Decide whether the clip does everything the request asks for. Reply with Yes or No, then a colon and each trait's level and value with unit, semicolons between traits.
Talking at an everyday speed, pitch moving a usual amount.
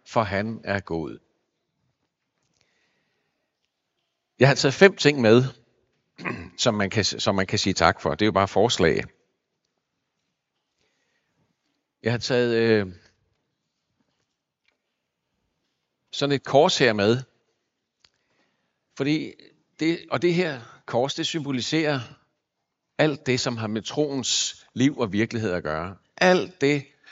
No: slow, 120 wpm; average, 4.9 semitones